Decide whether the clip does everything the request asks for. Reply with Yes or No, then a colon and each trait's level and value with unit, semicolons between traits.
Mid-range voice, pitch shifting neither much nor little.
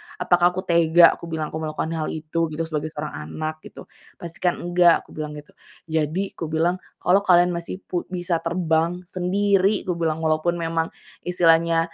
No: medium, 165 Hz; narrow, 2.0 semitones